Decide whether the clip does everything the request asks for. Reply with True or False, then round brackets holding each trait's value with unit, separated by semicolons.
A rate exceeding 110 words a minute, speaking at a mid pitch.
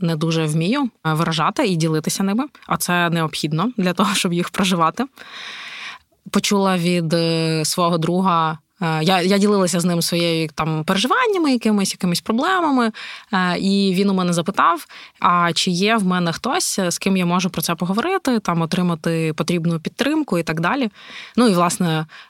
True (155 wpm; 180 Hz)